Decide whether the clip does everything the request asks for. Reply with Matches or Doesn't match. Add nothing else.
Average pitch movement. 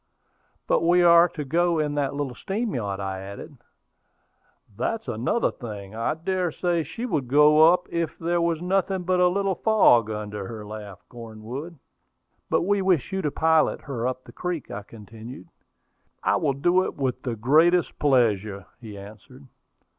Doesn't match